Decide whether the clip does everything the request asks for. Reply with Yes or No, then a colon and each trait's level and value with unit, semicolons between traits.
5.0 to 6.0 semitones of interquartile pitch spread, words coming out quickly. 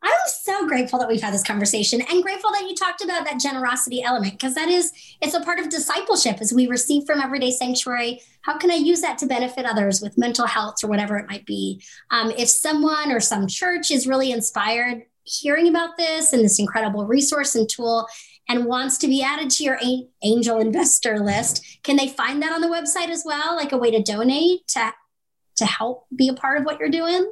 Yes: wide, 5.6 semitones; fast, 215 wpm